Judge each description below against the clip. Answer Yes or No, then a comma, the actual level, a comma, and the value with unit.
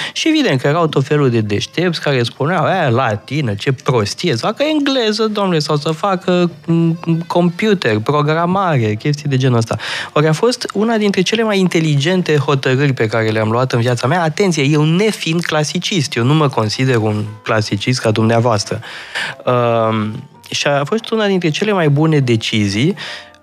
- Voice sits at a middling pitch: Yes, medium, 150 Hz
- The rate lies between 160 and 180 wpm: Yes, average, 165 wpm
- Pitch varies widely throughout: Yes, wide, 6.8 semitones